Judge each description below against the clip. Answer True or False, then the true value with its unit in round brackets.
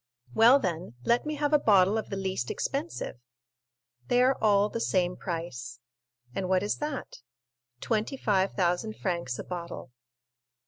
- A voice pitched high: True (195 Hz)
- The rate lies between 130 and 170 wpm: True (150 wpm)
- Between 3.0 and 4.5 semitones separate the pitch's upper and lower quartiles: False (5.1 semitones)